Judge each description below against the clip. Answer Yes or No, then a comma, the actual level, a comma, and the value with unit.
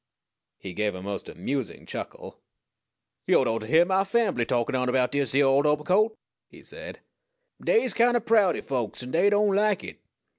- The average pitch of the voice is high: No, medium, 145 Hz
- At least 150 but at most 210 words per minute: Yes, average, 180 wpm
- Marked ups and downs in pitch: Yes, wide, 8.6 semitones